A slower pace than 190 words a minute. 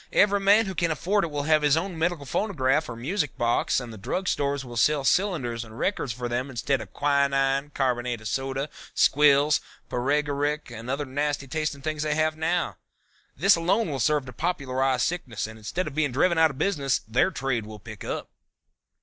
No: average, 195 wpm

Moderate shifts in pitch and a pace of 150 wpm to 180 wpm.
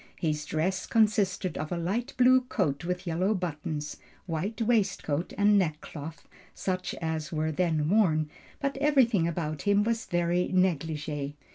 No: average, 4.8 semitones; average, 140 wpm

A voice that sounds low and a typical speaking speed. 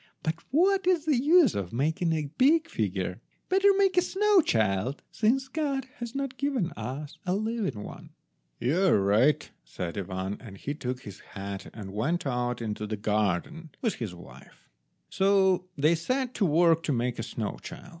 No: medium, 160 Hz; average, 175 wpm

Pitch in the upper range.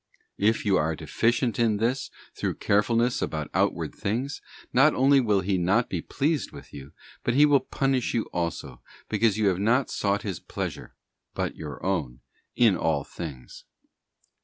No: low, 105 Hz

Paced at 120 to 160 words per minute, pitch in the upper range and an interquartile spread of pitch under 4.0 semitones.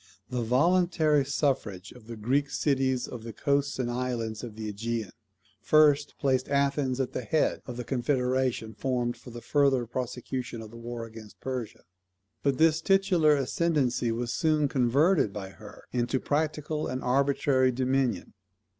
No: average, 155 wpm; low, 130 Hz; average, 3.2 semitones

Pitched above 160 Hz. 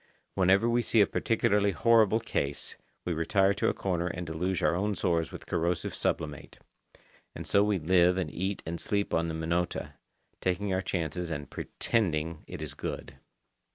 No: very low, 90 Hz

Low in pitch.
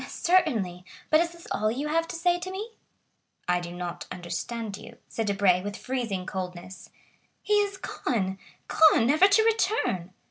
No: high, 230 Hz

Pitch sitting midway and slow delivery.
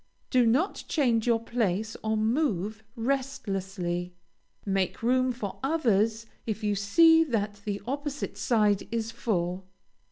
No: high, 225 Hz; slow, 125 wpm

